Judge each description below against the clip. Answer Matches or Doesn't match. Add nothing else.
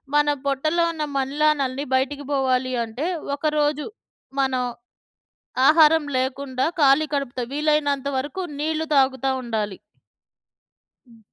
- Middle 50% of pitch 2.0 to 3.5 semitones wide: Matches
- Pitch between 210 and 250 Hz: Doesn't match